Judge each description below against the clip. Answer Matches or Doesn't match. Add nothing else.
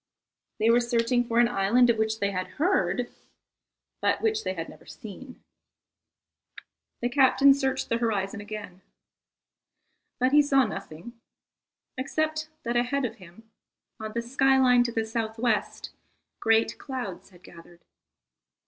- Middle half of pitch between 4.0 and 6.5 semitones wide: Doesn't match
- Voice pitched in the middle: Doesn't match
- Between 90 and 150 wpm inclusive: Matches